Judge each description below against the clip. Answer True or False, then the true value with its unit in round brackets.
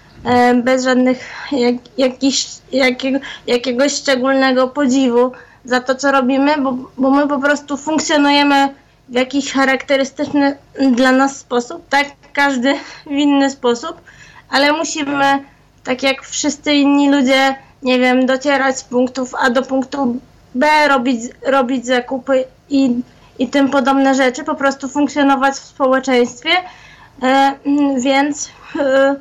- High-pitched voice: True (270 Hz)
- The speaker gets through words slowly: False (125 wpm)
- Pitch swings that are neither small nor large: False (1.5 semitones)